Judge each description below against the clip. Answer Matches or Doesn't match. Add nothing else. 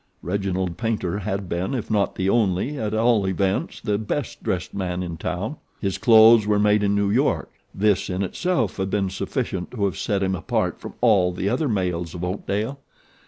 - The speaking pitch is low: Matches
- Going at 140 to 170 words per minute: Doesn't match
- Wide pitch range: Doesn't match